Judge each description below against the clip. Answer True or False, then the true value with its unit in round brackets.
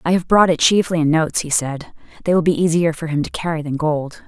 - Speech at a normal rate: False (265 wpm)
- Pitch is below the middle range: False (165 Hz)